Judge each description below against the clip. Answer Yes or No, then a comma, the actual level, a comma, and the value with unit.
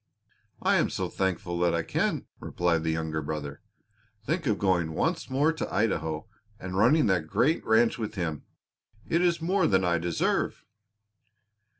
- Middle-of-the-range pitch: No, very low, 95 Hz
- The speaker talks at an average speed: Yes, average, 160 wpm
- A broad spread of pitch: Yes, wide, 8.4 semitones